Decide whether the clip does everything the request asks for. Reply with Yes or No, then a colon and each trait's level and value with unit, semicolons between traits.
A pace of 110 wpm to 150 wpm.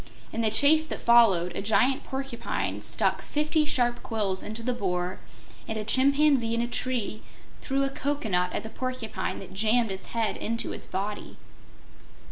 No: average, 165 wpm